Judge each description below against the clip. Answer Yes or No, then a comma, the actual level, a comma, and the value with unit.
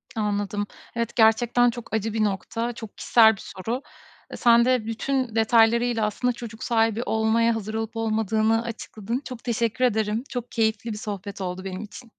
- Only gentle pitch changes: Yes, narrow, 1.6 semitones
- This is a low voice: No, high, 225 Hz